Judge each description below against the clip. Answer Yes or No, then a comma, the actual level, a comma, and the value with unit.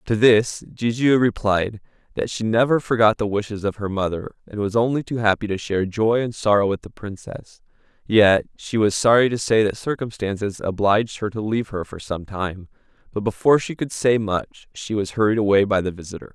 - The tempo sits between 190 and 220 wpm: Yes, average, 200 wpm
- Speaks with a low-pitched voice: Yes, low, 105 Hz